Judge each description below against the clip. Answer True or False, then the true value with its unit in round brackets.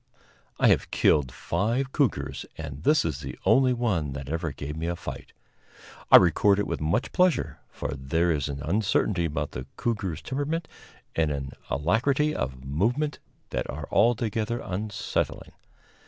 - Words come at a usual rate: True (155 wpm)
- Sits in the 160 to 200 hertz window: False (90 Hz)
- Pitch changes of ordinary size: False (8.2 semitones)